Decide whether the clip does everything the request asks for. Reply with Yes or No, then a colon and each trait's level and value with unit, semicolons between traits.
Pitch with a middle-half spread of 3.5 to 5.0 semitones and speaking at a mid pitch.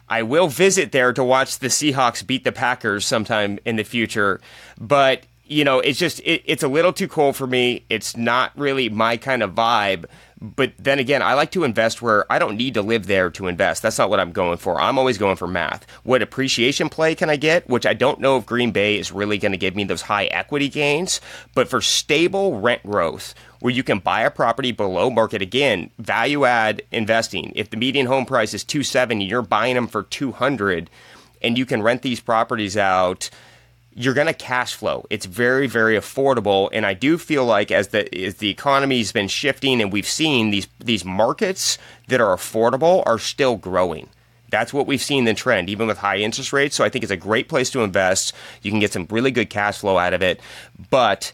No: average, 4.1 semitones; low, 120 Hz